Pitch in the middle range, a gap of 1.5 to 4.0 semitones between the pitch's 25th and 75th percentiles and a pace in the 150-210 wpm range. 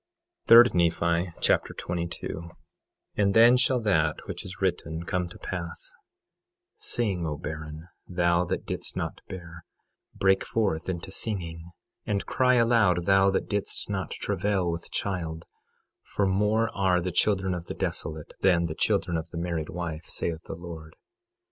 No: very low, 90 Hz; average, 2.8 semitones; average, 155 wpm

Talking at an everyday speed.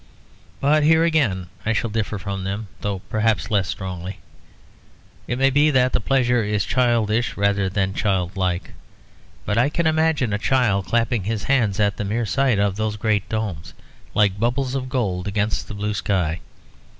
Yes: average, 170 wpm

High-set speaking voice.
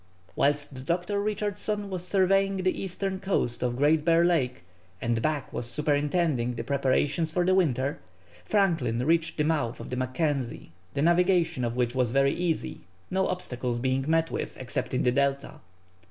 No: medium, 150 Hz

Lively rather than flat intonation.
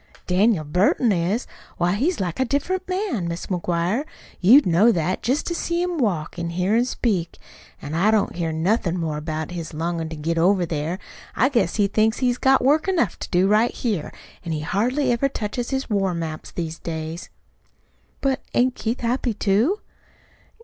Yes: wide, 6.6 semitones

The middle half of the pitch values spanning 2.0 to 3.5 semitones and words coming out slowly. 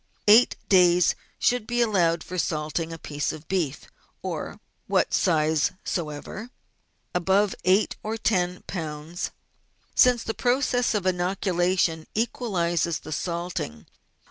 No: average, 4.3 semitones; slow, 115 wpm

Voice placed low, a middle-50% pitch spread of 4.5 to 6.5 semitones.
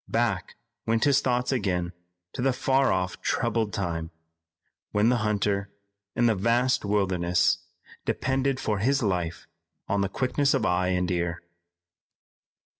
Yes: low, 105 Hz; wide, 5.5 semitones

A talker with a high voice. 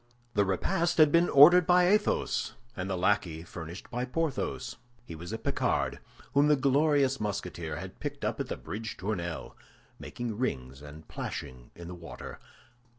No: low, 105 Hz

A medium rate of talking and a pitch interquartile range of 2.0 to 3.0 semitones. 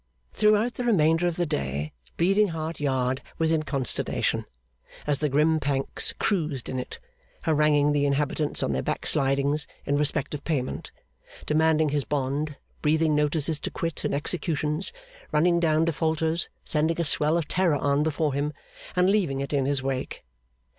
Yes: average, 160 wpm; narrow, 2.4 semitones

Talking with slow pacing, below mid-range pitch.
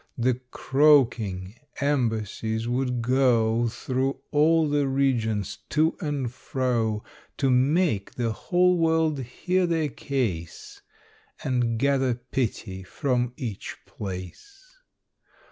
Yes: slow, 100 wpm; low, 125 Hz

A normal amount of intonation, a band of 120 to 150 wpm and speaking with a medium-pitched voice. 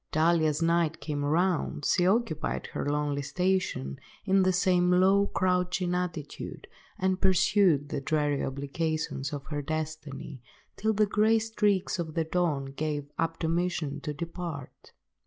Yes: average, 3.8 semitones; average, 140 wpm; medium, 165 Hz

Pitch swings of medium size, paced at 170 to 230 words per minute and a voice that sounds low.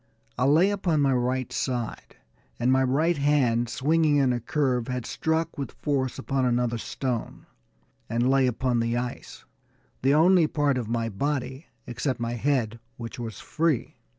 No: average, 3.3 semitones; average, 160 wpm; low, 130 Hz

